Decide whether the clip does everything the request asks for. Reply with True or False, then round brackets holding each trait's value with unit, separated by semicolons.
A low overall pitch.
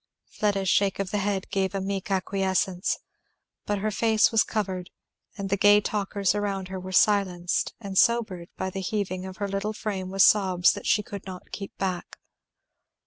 False (195 Hz)